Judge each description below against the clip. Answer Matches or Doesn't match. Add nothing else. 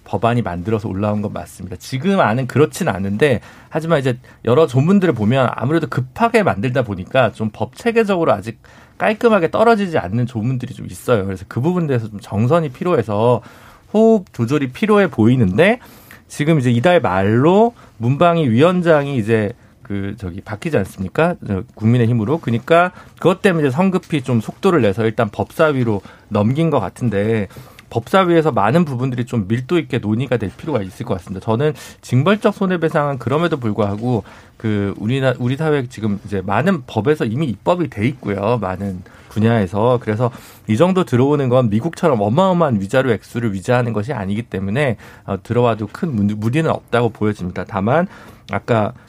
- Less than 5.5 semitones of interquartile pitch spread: Doesn't match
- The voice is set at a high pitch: Doesn't match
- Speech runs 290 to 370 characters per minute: Doesn't match